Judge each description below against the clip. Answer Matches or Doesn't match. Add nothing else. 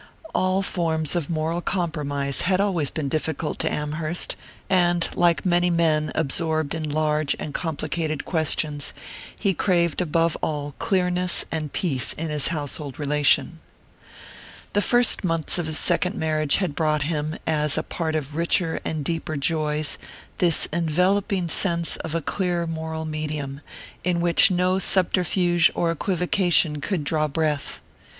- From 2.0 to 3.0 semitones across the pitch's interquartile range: Matches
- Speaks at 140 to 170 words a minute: Matches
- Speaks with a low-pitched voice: Doesn't match